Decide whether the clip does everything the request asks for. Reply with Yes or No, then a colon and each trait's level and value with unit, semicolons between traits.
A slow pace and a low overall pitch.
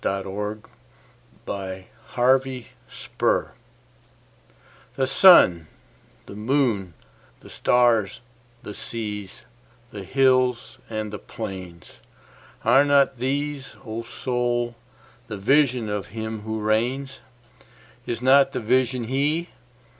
Yes: slow, 90 wpm; low, 120 Hz